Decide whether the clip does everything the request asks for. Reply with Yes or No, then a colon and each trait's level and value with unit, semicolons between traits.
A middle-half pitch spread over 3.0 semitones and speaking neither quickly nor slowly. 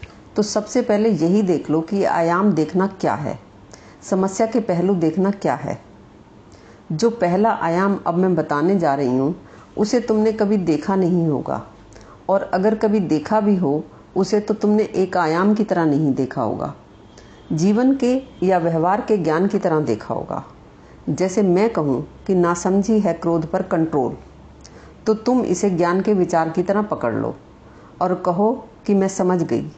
Yes: average, 4.8 semitones; average, 165 wpm